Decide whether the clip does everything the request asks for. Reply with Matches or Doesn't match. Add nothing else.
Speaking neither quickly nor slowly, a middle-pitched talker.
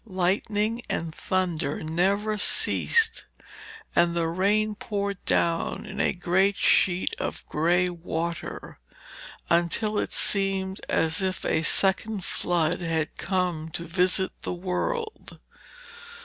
Doesn't match